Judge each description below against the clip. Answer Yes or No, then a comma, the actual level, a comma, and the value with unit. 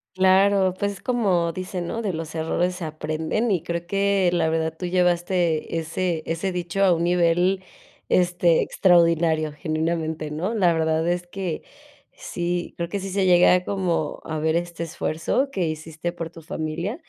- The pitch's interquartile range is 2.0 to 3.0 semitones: Yes, narrow, 2.4 semitones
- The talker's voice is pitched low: No, medium, 175 Hz